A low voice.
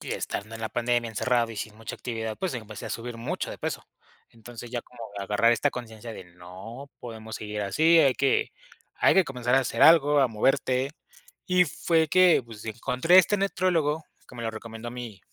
Yes: low, 120 Hz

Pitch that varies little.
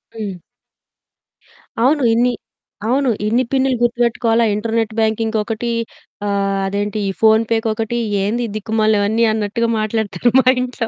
Yes: narrow, 1.9 semitones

